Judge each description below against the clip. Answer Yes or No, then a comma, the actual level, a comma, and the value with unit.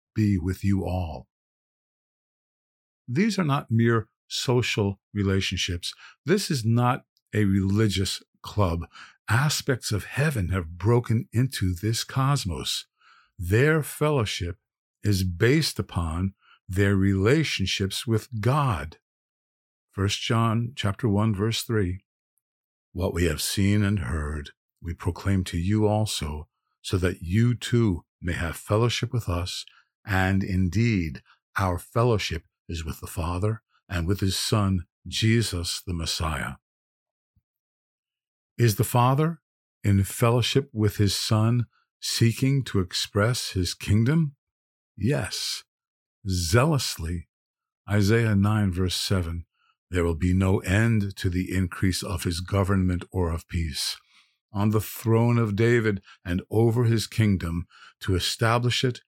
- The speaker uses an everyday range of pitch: Yes, average, 4.1 semitones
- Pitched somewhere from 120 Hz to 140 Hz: No, low, 100 Hz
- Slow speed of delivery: Yes, slow, 120 wpm